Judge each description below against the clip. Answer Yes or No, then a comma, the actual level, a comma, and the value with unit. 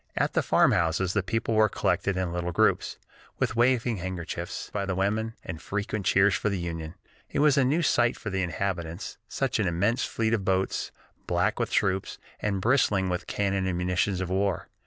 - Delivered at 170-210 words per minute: Yes, average, 190 wpm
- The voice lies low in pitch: Yes, very low, 95 Hz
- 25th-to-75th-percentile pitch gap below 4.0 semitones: Yes, average, 3.4 semitones